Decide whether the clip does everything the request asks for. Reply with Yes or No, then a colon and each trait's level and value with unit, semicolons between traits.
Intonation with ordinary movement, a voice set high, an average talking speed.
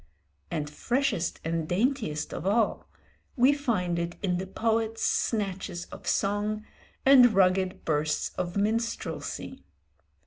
No: average, 4.6 semitones; high, 200 Hz; slow, 115 wpm